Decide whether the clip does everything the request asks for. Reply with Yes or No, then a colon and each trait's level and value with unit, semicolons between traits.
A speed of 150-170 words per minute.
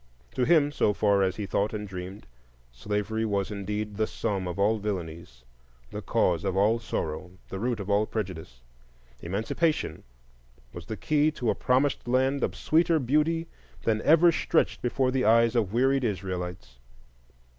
Yes: average, 160 wpm